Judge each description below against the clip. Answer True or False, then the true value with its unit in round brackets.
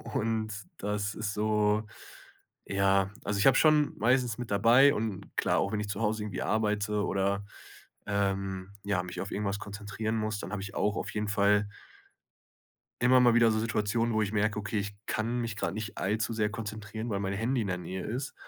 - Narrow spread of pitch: True (1.7 semitones)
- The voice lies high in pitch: False (105 Hz)